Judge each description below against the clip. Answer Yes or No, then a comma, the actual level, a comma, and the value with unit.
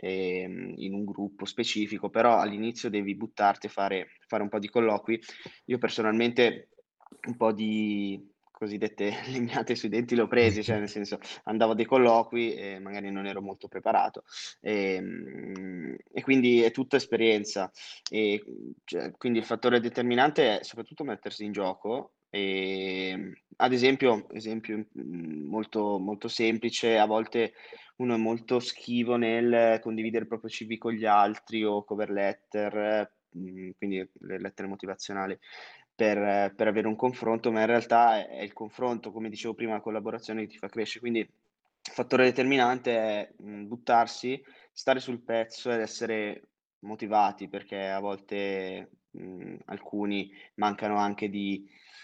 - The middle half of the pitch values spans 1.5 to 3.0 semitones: Yes, narrow, 2.5 semitones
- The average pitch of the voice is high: No, low, 110 Hz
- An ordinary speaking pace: Yes, average, 140 wpm